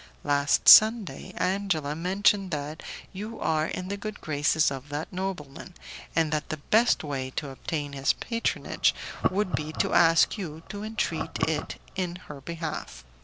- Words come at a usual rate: Yes, average, 155 wpm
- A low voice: No, medium, 165 Hz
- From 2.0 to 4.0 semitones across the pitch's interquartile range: No, average, 4.7 semitones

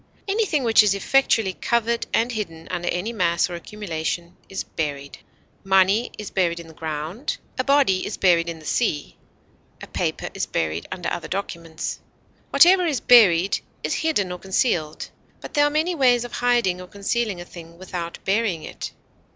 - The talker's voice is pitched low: No, high, 190 Hz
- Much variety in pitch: Yes, wide, 5.7 semitones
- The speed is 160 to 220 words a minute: Yes, average, 170 wpm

